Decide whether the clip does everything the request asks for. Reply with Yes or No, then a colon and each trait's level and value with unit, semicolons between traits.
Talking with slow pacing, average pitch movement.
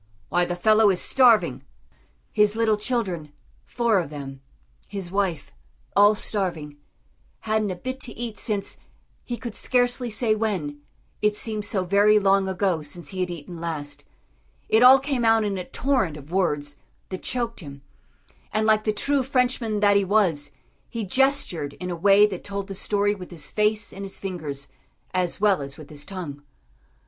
No: average, 175 wpm; average, 4.1 semitones